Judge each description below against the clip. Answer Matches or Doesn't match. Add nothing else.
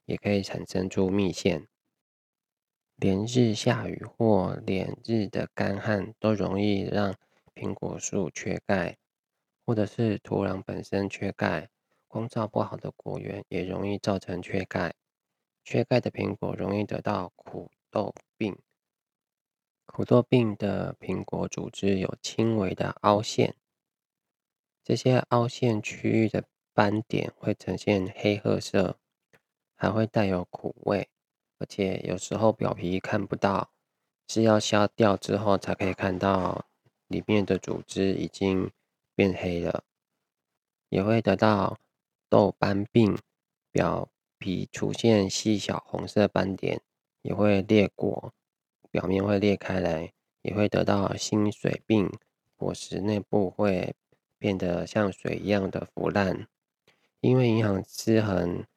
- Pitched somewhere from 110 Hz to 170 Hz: Doesn't match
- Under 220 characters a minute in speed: Matches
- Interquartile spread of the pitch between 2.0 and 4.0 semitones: Matches